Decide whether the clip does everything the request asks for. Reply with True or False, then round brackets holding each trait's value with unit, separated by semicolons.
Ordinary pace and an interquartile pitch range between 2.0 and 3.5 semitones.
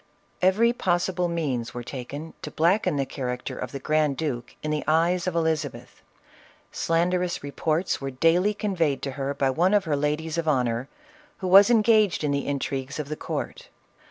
False (175 wpm; 4.4 semitones)